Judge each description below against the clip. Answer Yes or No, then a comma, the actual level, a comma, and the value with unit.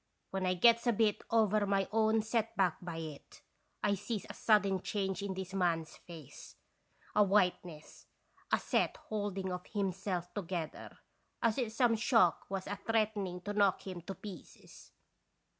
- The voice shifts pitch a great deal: No, average, 2.8 semitones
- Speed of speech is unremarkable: Yes, average, 165 wpm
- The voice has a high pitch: Yes, high, 195 Hz